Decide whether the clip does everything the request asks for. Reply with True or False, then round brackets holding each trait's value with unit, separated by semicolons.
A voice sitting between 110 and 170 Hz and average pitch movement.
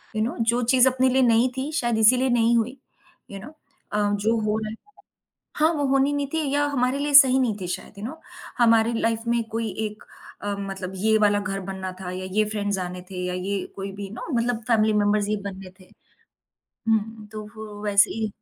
False (220 Hz; 3.2 semitones)